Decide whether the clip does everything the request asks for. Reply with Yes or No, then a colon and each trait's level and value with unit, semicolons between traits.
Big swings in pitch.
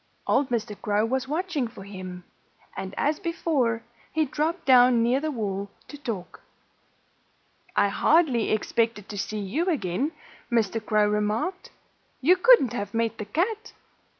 Yes: wide, 6.5 semitones